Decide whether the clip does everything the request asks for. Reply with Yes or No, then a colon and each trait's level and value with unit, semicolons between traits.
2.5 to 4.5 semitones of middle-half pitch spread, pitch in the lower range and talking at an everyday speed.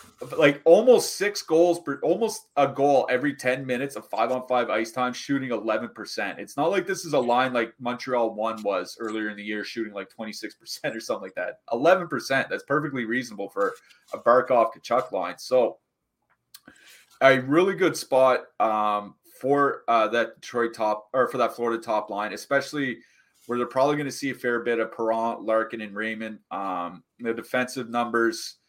Yes: average, 3.5 semitones; low, 120 Hz; average, 180 wpm